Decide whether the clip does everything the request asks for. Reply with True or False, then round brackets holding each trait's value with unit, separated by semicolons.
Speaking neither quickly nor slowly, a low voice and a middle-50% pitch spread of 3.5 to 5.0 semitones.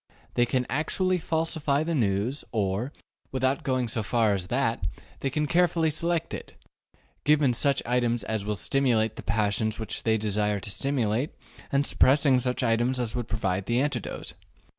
True (160 wpm; 125 Hz; 4.5 semitones)